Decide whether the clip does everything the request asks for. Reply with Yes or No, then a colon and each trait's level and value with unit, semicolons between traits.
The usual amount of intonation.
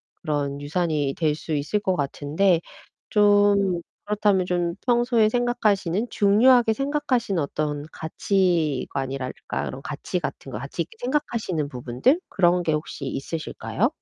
No: wide, 6.1 semitones